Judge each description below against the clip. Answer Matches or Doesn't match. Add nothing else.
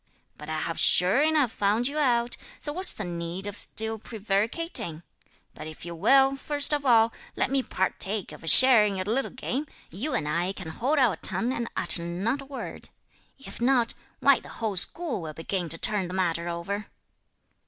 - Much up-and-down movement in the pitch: Matches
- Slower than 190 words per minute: Doesn't match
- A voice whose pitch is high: Matches